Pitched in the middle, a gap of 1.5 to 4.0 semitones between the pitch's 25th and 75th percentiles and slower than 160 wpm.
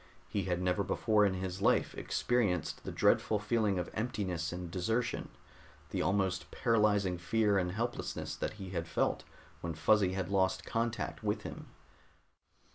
No: very low, 95 Hz; average, 3.2 semitones; average, 150 wpm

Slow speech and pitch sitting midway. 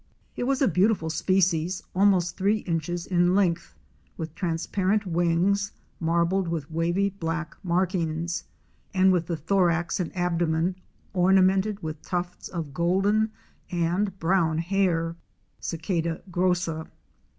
Yes: slow, 115 wpm; medium, 175 Hz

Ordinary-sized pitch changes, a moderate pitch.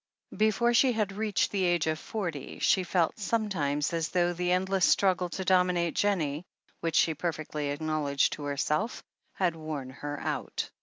Yes: average, 4.0 semitones; medium, 175 Hz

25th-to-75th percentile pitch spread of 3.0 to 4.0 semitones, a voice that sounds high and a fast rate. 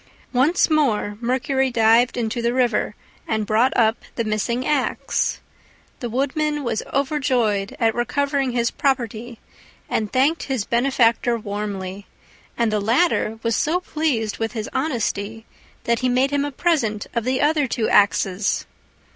No: average, 3.7 semitones; high, 240 Hz; average, 145 wpm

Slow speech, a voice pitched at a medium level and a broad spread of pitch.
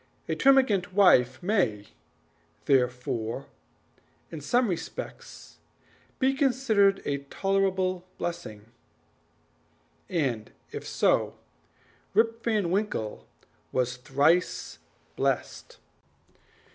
Yes: slow, 80 wpm; medium, 180 Hz; wide, 8.5 semitones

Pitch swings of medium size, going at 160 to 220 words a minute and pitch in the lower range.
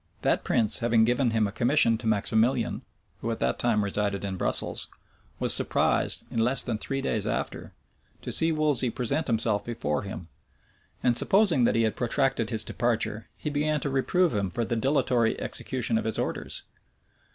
Yes: average, 3.4 semitones; average, 175 wpm; low, 115 Hz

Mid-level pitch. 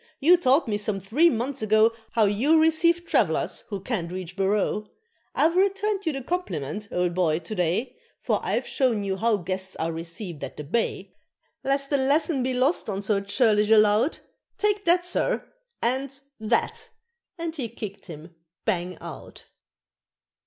No: high, 225 Hz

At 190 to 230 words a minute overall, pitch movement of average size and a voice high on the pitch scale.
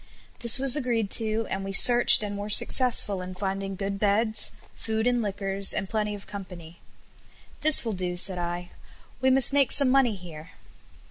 No: average, 175 wpm; average, 3.7 semitones; high, 205 Hz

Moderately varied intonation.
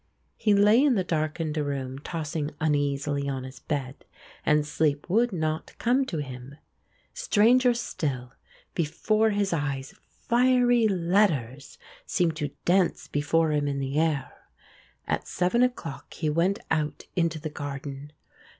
No: wide, 5.8 semitones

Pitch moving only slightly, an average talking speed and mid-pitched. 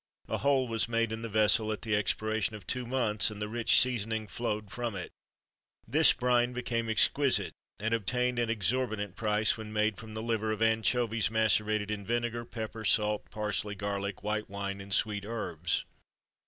No: narrow, 1.8 semitones; average, 180 wpm; low, 110 Hz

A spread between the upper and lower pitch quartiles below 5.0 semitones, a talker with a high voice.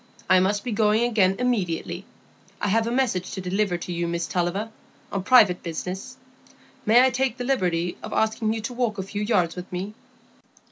Yes: average, 4.1 semitones; high, 205 Hz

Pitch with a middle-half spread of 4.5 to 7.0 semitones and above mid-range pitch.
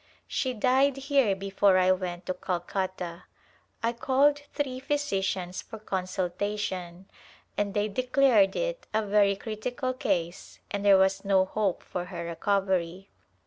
Yes: average, 5.2 semitones; high, 200 Hz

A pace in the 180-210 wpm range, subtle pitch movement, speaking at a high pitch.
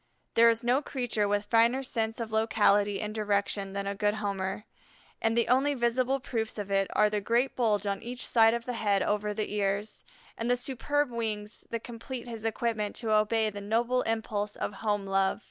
Yes: average, 195 wpm; narrow, 2.3 semitones; high, 220 Hz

